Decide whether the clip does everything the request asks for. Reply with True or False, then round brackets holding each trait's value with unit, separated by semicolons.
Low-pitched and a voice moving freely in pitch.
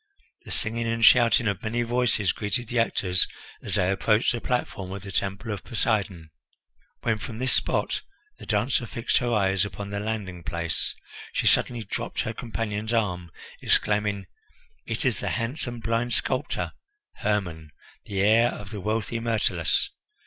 False (105 Hz; 2.9 semitones)